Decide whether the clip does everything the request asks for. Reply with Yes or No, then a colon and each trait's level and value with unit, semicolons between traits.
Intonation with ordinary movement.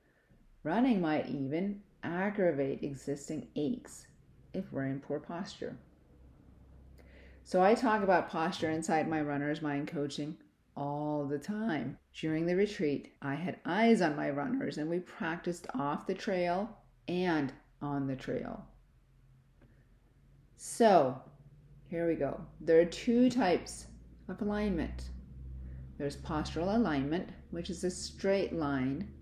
Yes: average, 4.8 semitones